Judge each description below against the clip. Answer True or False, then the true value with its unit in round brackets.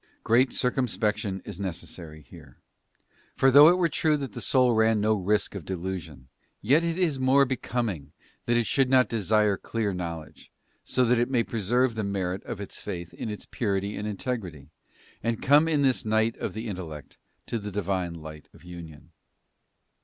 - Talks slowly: False (180 wpm)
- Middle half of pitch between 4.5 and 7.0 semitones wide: True (5.4 semitones)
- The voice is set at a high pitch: False (105 Hz)